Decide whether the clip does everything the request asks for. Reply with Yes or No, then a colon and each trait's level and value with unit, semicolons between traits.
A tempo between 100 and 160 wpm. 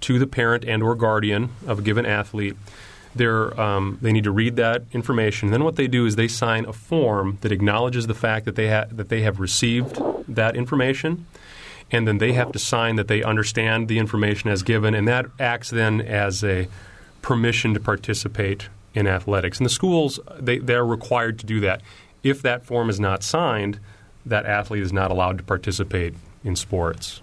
No: average, 195 wpm